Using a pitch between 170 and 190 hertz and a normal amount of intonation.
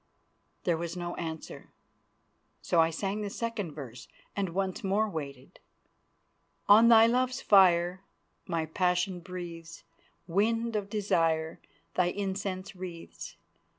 Yes: medium, 185 Hz; average, 3.4 semitones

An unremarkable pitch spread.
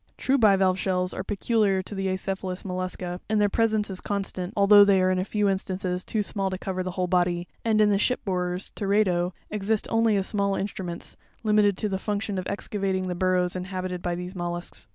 No: narrow, 2.1 semitones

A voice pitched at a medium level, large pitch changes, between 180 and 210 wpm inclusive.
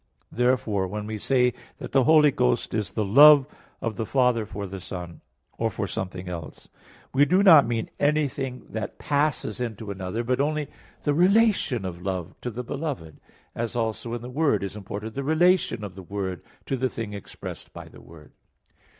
No: low, 115 Hz; wide, 5.8 semitones; average, 185 wpm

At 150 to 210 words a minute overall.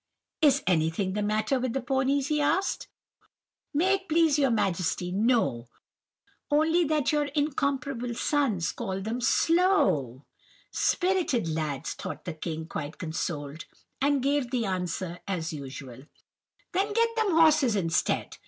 No: slow, 135 wpm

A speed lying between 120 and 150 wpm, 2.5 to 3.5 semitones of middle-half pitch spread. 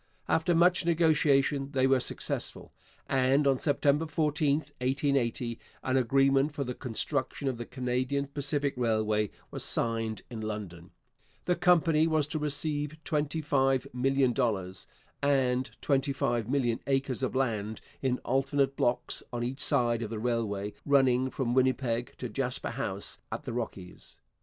Yes: slow, 135 wpm; average, 3.1 semitones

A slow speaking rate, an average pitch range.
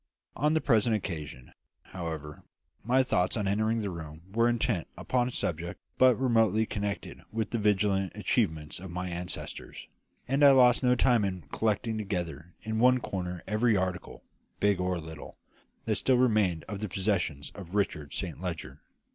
No: average, 165 wpm; average, 4.6 semitones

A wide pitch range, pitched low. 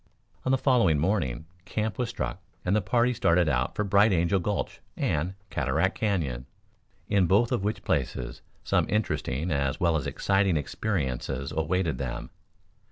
Yes: wide, 6.3 semitones; very low, 90 Hz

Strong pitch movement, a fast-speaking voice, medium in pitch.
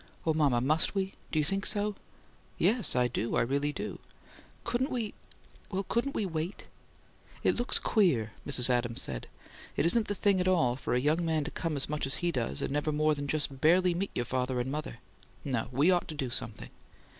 Yes: wide, 6.1 semitones; fast, 210 wpm; medium, 155 Hz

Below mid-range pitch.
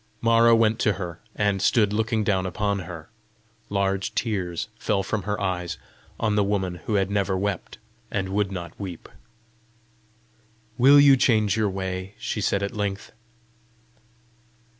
Yes: low, 100 Hz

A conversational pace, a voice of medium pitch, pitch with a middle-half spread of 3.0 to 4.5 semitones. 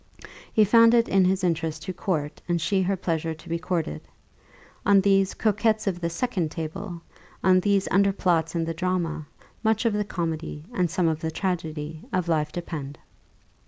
Yes: average, 170 wpm; medium, 175 Hz; average, 3.3 semitones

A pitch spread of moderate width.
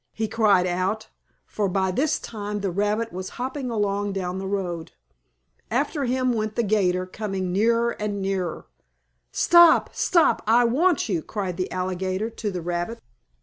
Yes: average, 3.7 semitones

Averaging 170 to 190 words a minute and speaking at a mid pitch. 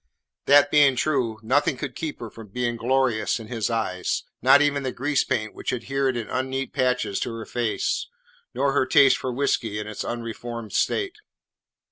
No: average, 175 wpm; low, 125 Hz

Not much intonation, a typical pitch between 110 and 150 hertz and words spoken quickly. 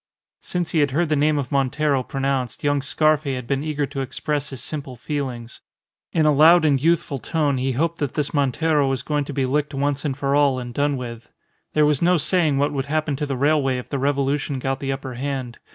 Yes: narrow, 2.0 semitones; medium, 140 Hz; fast, 220 wpm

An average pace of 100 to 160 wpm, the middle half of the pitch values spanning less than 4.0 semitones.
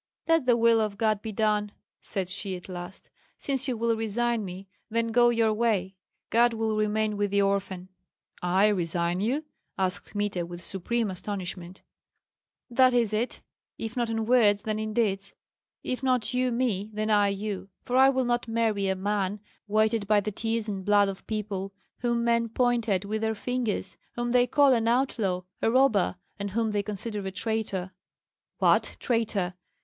No: average, 175 wpm; average, 2.9 semitones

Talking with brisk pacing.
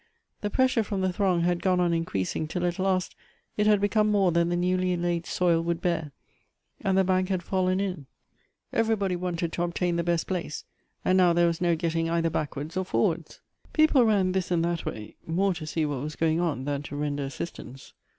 Yes: fast, 210 wpm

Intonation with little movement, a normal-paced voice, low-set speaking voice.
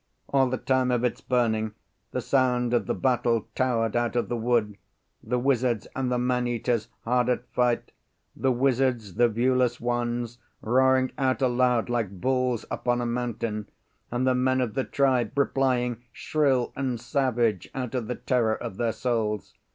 Yes: narrow, 1.7 semitones; average, 165 wpm; low, 120 Hz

